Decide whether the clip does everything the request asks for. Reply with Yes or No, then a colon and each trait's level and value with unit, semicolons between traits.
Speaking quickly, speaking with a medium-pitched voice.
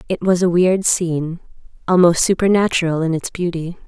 No: average, 155 wpm; medium, 175 Hz